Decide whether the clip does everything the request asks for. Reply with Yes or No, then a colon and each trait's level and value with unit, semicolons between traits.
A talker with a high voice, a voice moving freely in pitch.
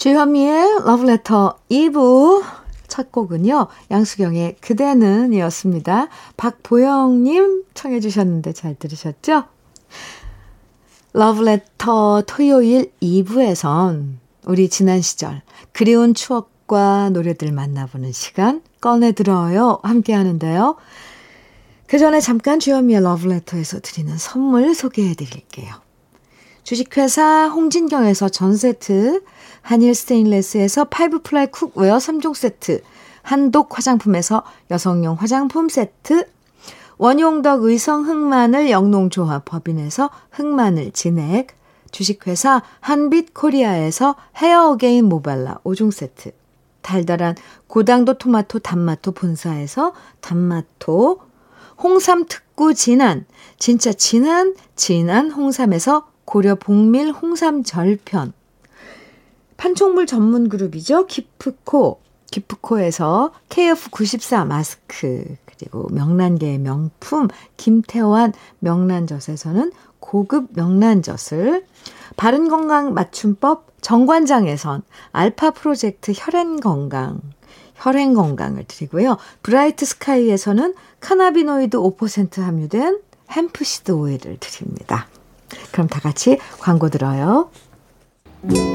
Yes: high, 225 Hz; wide, 7.8 semitones